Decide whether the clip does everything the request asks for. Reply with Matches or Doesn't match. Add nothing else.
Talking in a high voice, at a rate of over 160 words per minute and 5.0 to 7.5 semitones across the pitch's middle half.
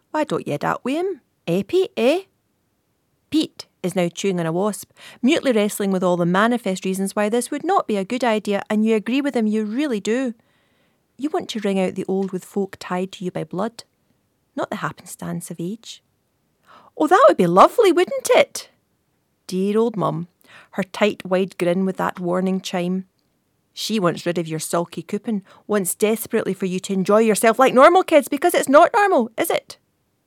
Matches